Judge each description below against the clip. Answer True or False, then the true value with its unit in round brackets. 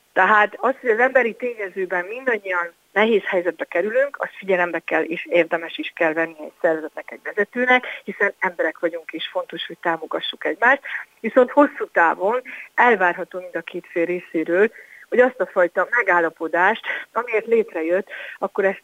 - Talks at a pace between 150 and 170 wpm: True (155 wpm)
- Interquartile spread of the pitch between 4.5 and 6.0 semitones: True (5.0 semitones)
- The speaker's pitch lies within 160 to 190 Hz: True (185 Hz)